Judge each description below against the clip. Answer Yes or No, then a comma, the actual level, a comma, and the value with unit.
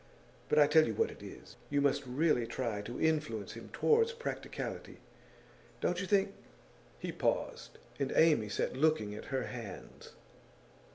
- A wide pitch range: Yes, wide, 5.8 semitones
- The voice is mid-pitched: Yes, medium, 145 Hz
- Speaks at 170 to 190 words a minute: No, average, 160 wpm